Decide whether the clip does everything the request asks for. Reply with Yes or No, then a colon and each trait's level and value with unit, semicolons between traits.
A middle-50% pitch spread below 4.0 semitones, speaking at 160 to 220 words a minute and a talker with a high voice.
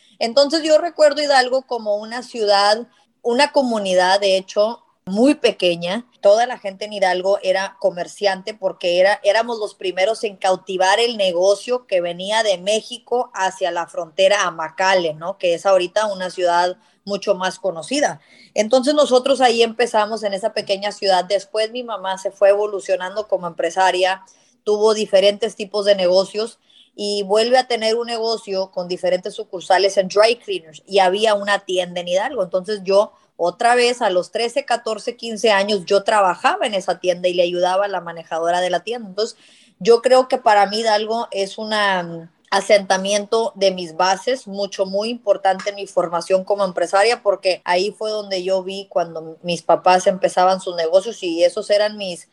Yes: average, 3.3 semitones; average, 170 wpm; high, 200 Hz